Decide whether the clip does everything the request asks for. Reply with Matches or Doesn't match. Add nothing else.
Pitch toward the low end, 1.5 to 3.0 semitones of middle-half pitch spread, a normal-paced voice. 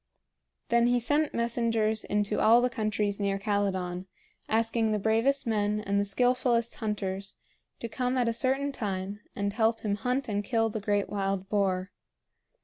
Doesn't match